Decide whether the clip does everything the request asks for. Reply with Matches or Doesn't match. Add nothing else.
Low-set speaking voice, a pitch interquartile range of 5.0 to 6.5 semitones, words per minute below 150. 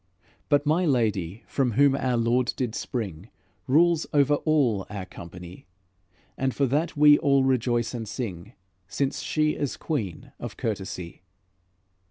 Matches